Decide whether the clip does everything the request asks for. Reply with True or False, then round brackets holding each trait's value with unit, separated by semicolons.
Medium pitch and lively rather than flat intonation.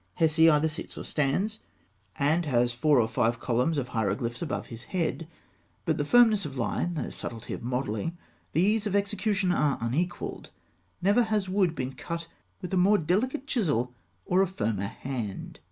True (160 Hz; 7.3 semitones)